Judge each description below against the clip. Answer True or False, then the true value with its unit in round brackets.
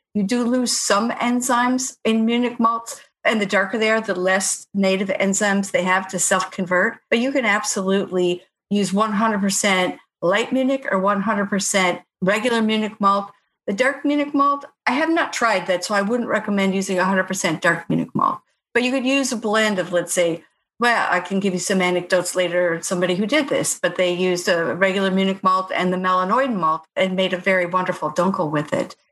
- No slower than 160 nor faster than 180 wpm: False (190 wpm)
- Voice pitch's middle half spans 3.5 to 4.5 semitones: True (3.8 semitones)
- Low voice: False (195 Hz)